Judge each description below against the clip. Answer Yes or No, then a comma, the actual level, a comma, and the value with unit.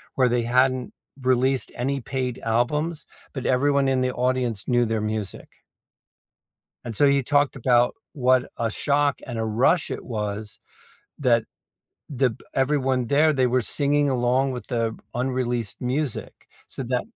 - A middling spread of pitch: No, narrow, 2.3 semitones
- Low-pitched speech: Yes, low, 125 Hz